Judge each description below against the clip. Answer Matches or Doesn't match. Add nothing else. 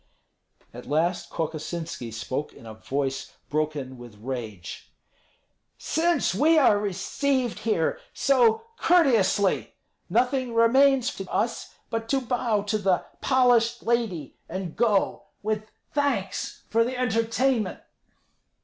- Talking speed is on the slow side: Matches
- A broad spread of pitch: Matches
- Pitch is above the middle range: Matches